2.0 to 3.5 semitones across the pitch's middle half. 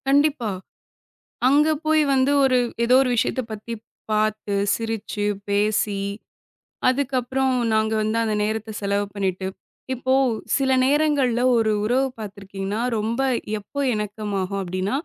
No: average, 4.1 semitones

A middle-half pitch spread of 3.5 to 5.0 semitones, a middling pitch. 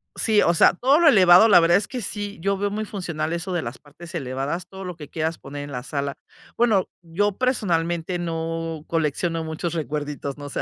Yes: average, 4.1 semitones; medium, 170 Hz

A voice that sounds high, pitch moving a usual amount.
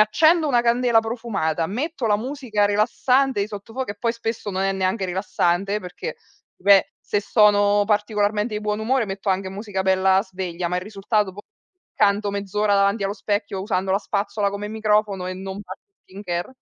No: high, 205 Hz; narrow, 2.2 semitones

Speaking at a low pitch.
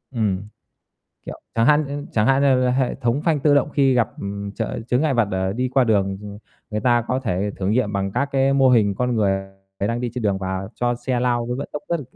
Yes: low, 120 Hz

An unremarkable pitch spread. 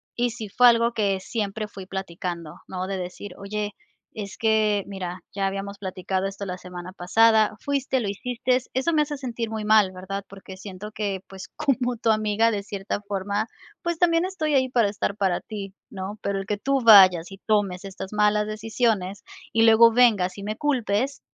Yes: average, 3.1 semitones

